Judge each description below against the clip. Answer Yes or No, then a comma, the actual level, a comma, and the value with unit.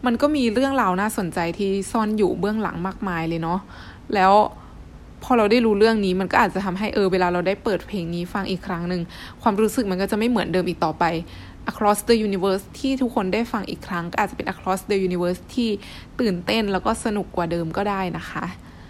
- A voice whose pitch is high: Yes, high, 195 Hz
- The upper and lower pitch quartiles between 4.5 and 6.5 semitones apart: No, average, 3.6 semitones